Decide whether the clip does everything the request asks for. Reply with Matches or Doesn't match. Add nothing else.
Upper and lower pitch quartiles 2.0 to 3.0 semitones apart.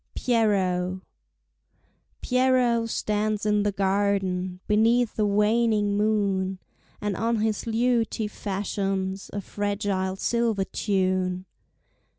Matches